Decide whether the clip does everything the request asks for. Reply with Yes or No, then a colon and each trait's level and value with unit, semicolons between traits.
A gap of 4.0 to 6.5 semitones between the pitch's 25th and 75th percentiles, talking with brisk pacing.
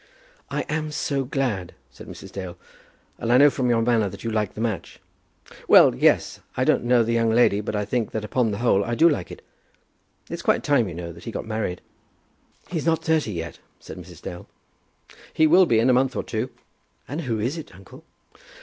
Yes: average, 4.5 semitones; fast, 215 wpm